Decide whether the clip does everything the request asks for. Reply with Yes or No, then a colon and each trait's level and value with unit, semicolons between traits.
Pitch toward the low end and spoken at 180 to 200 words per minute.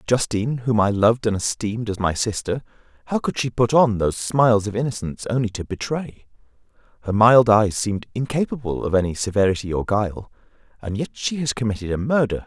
Yes: low, 110 Hz; average, 185 wpm